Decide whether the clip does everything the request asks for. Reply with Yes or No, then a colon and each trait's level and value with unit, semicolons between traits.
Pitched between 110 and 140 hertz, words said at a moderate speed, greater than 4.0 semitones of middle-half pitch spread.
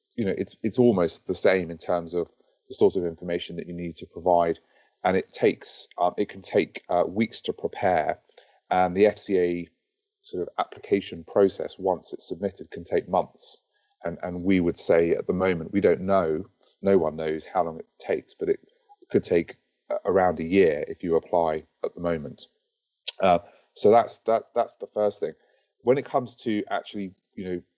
No: very low, 95 Hz; average, 190 wpm; average, 4.8 semitones